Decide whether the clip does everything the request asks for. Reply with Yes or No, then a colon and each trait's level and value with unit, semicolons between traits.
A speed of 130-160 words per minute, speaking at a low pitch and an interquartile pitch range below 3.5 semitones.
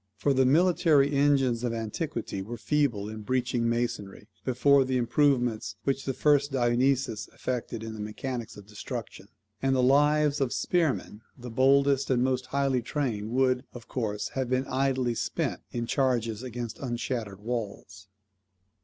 Yes: average, 150 wpm; low, 125 Hz; average, 2.9 semitones